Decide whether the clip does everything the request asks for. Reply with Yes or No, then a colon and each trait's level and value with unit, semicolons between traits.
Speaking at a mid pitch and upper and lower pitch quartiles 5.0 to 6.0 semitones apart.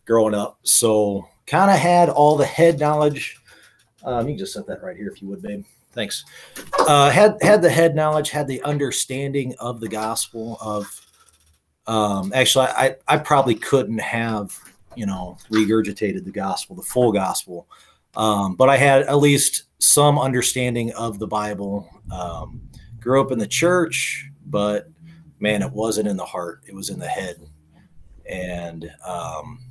No: low, 115 Hz; wide, 5.5 semitones